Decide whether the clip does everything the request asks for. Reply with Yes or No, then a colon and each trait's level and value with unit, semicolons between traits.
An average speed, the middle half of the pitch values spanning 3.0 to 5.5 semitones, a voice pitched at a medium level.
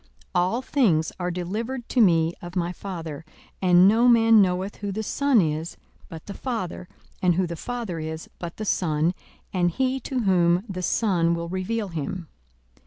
Yes: average, 175 wpm; average, 4.4 semitones; medium, 180 Hz